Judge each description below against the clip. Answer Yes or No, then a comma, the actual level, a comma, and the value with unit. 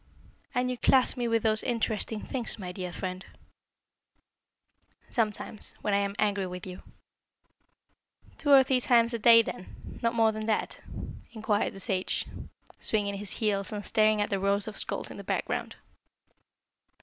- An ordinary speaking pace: Yes, average, 160 wpm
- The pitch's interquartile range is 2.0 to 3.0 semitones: Yes, narrow, 2.6 semitones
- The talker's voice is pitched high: Yes, high, 215 Hz